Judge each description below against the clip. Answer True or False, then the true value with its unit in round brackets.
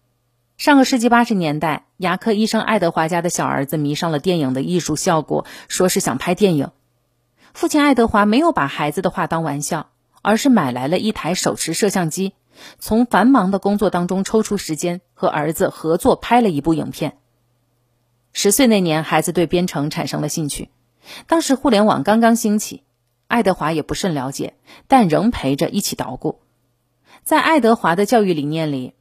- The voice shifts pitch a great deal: True (6.5 semitones)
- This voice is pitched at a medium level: True (175 Hz)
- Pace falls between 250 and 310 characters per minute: True (280 characters per minute)